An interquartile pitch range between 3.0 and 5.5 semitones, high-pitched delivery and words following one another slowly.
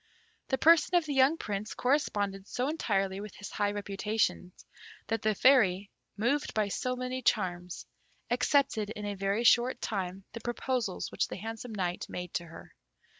No: average, 4.3 semitones; high, 215 Hz; average, 165 wpm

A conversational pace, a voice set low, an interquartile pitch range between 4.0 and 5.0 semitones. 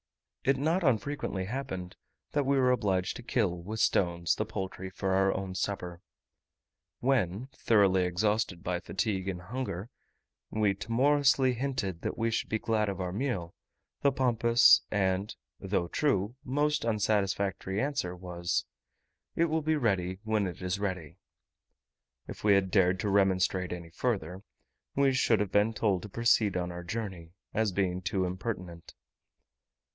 Yes: average, 150 wpm; low, 100 Hz; average, 4.3 semitones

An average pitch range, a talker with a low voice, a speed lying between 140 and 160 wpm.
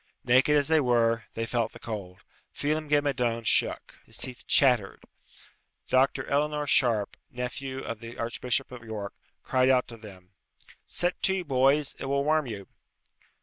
Yes: average, 3.7 semitones; low, 125 Hz; average, 155 wpm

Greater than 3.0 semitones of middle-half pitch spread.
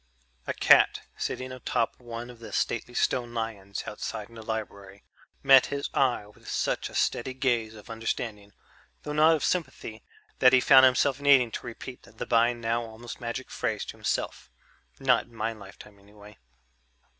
No: average, 2.7 semitones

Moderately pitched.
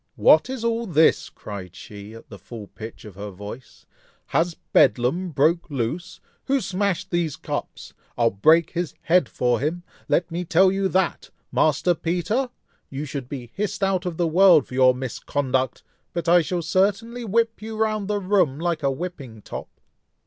Yes: medium, 170 Hz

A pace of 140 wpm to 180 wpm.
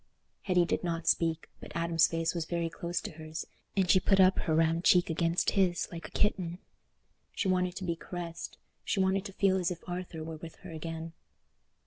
No: average, 195 wpm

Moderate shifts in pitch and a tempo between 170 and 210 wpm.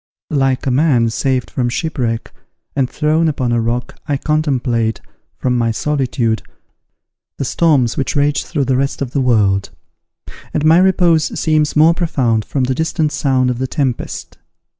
No: average, 3.8 semitones; average, 160 wpm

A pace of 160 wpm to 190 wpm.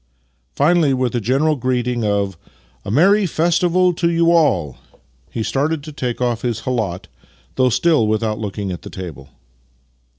Yes: average, 170 wpm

